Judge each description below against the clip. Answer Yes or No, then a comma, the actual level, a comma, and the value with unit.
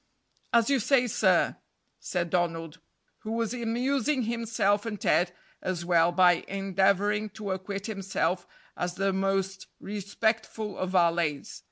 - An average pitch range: Yes, average, 3.6 semitones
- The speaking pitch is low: No, high, 195 Hz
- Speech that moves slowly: Yes, slow, 130 wpm